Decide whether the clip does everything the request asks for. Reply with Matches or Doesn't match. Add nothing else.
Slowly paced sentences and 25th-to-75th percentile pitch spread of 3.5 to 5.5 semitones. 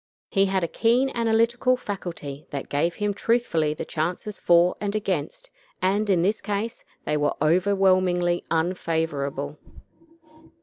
Matches